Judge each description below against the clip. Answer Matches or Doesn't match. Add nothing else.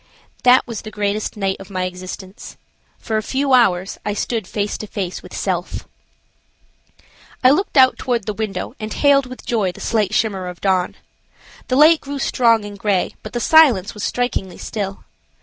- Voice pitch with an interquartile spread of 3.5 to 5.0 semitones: Matches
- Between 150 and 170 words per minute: Doesn't match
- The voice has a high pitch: Matches